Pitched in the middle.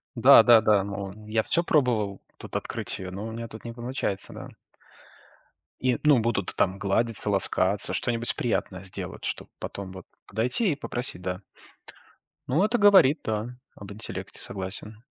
No: low, 110 Hz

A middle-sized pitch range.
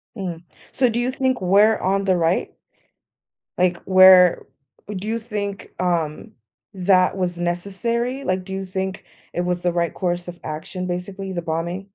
No: narrow, 2.2 semitones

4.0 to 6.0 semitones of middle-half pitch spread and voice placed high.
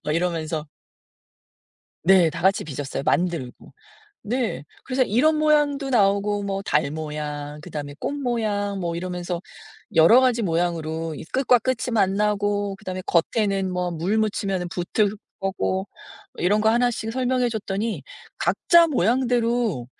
Yes: wide, 5.5 semitones; high, 200 Hz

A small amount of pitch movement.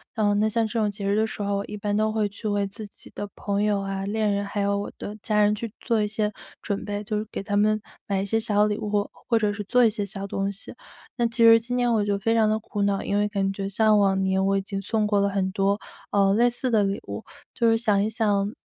Yes: narrow, 1.5 semitones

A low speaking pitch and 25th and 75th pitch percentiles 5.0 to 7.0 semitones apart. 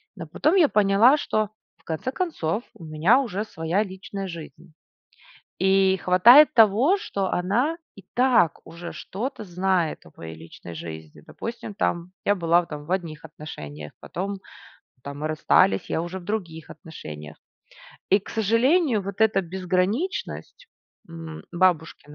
No: medium, 185 Hz; average, 5.3 semitones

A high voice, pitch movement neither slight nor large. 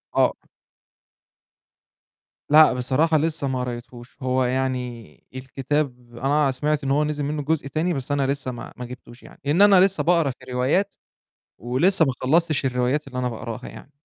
No: low, 135 Hz; average, 3.3 semitones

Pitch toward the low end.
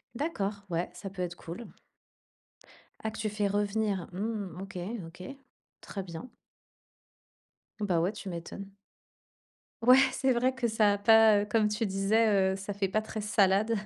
No: high, 205 Hz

